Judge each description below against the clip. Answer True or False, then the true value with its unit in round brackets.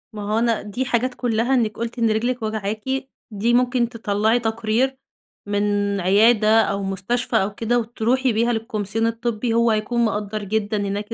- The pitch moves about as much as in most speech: False (2.3 semitones)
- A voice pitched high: True (225 Hz)